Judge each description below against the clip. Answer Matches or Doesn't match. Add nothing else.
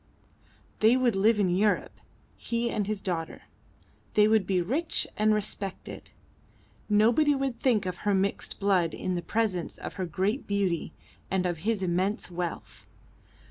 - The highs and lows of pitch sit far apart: Doesn't match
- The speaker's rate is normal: Matches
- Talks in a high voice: Matches